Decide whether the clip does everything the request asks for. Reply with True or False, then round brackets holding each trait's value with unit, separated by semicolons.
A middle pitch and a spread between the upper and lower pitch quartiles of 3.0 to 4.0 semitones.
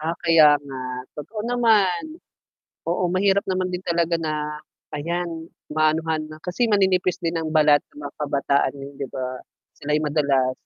True (160 Hz; 3.5 semitones)